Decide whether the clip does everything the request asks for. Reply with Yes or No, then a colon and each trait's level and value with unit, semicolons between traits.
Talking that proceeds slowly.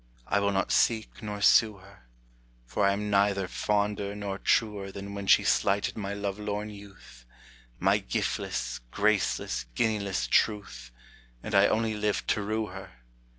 No: average, 145 wpm